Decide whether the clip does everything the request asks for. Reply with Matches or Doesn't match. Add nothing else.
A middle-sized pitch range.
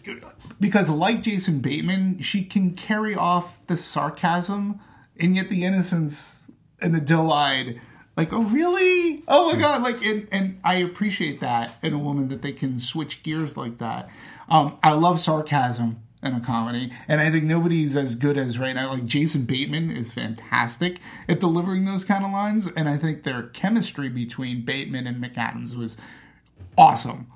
Doesn't match